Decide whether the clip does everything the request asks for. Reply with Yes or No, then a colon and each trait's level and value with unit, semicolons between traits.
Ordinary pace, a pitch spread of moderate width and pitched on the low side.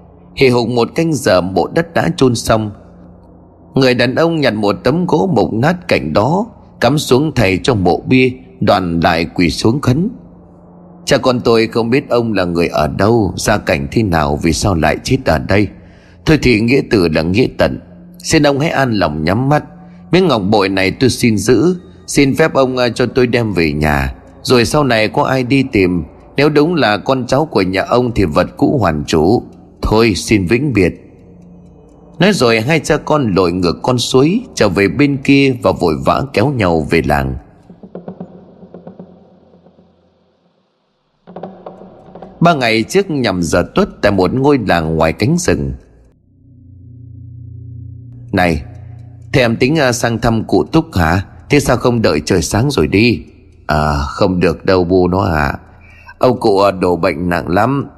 No: average, 175 wpm; wide, 8.1 semitones; low, 115 Hz